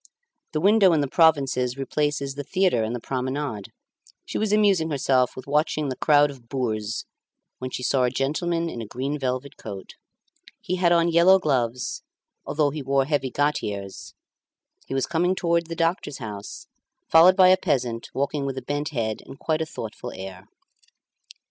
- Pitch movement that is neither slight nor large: Yes, average, 4.4 semitones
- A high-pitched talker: No, medium, 140 Hz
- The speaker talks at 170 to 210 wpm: Yes, average, 175 wpm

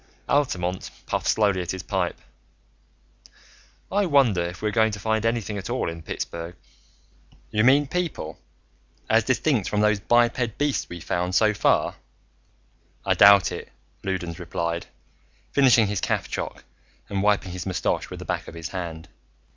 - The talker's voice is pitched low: Yes, low, 100 Hz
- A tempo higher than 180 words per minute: No, average, 150 wpm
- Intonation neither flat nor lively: Yes, average, 4.8 semitones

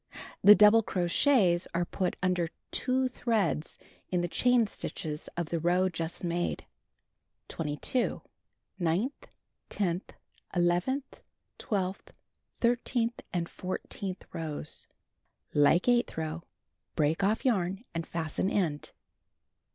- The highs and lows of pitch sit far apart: No, average, 4.7 semitones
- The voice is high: No, medium, 180 Hz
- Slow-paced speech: Yes, slow, 105 wpm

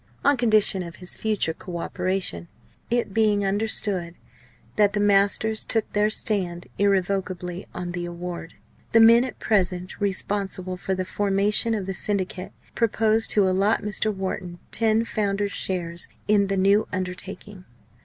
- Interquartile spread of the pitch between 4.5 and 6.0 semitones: No, narrow, 2.5 semitones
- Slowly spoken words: No, average, 145 wpm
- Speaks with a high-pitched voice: Yes, high, 195 Hz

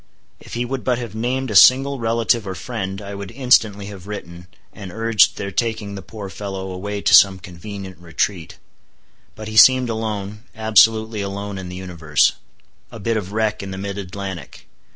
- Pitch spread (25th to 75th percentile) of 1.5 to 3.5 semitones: Yes, average, 2.9 semitones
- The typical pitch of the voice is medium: No, low, 100 Hz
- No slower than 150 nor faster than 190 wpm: Yes, average, 180 wpm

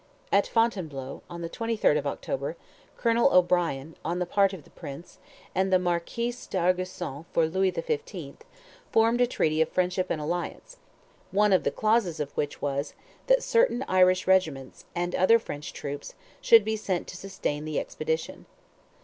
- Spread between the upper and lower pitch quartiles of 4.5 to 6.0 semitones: Yes, average, 5.1 semitones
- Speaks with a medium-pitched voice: Yes, medium, 180 Hz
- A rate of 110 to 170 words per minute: Yes, average, 160 wpm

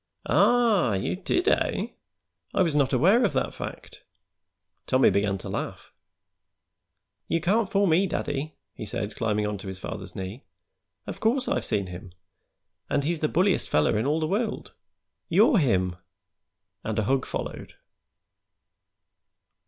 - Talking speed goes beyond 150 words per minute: No, average, 145 wpm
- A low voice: No, medium, 145 Hz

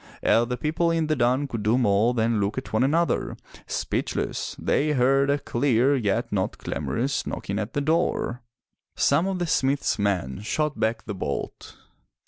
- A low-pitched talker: Yes, low, 125 Hz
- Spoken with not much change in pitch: No, average, 4.7 semitones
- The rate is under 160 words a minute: No, average, 170 wpm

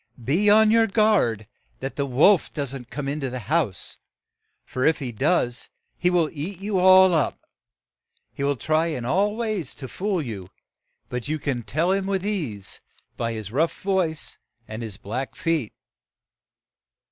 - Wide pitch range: Yes, wide, 7.2 semitones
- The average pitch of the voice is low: No, medium, 155 Hz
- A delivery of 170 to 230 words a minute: No, average, 160 wpm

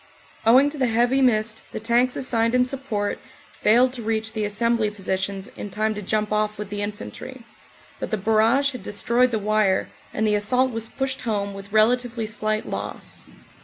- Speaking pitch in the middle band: No, high, 220 Hz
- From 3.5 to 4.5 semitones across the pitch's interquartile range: No, average, 2.8 semitones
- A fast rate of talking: No, average, 180 wpm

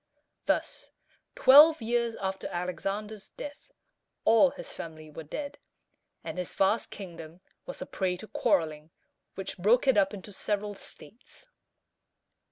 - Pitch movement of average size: Yes, average, 4.6 semitones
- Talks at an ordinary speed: No, slow, 130 wpm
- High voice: Yes, high, 200 Hz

